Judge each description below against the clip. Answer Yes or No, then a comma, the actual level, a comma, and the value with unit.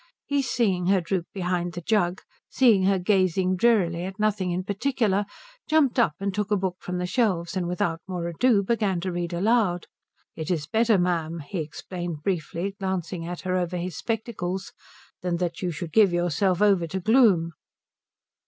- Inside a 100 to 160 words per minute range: No, average, 175 wpm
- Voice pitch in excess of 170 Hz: Yes, medium, 185 Hz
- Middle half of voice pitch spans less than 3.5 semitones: Yes, average, 2.9 semitones